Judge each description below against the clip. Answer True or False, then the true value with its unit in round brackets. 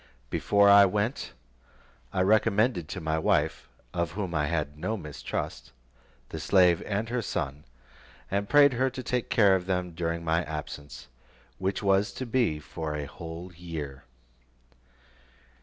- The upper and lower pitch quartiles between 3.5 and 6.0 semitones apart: True (4.5 semitones)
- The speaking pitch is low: True (90 Hz)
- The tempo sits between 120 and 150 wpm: True (145 wpm)